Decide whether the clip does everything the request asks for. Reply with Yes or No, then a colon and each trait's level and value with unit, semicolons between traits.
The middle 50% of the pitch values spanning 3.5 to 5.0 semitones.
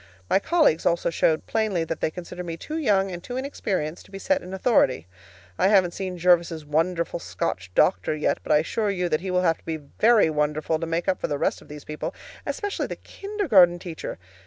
Yes: average, 3.8 semitones